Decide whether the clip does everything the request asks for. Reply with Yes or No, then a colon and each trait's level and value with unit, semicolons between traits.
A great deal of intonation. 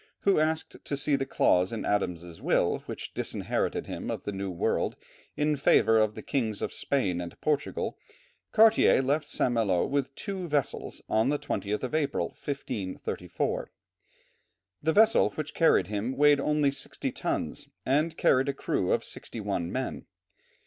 Yes: wide, 6.3 semitones